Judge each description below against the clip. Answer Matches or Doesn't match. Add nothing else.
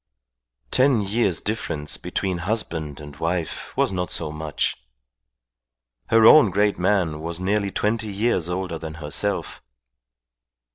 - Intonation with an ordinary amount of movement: Matches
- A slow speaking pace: Matches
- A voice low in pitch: Matches